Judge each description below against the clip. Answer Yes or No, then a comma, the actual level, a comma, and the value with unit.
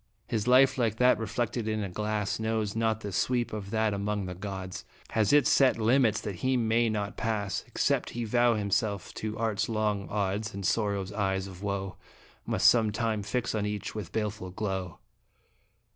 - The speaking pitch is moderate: No, low, 105 Hz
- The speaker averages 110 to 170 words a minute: No, average, 180 wpm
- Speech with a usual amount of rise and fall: No, narrow, 2.1 semitones